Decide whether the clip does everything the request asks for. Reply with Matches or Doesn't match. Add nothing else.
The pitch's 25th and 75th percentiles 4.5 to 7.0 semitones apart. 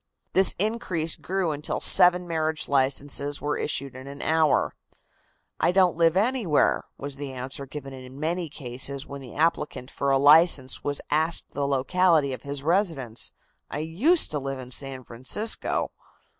Doesn't match